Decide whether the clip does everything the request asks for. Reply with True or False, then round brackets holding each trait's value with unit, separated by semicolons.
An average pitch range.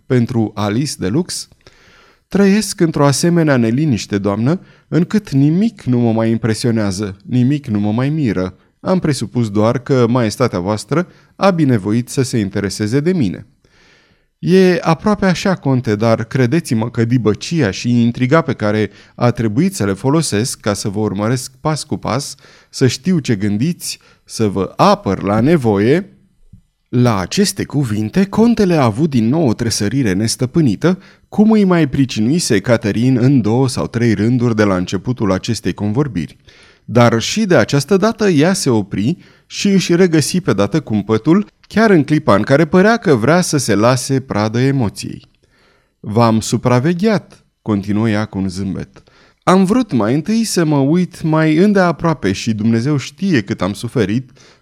False (7.1 semitones)